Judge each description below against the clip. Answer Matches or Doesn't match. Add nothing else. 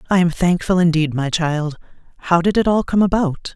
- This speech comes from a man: Doesn't match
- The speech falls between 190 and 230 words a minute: Matches